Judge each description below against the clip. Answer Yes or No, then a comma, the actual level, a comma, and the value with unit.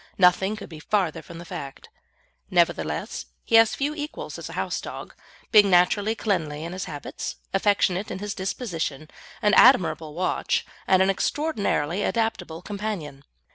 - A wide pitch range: No, average, 4.4 semitones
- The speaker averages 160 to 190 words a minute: No, average, 150 wpm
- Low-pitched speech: No, medium, 185 Hz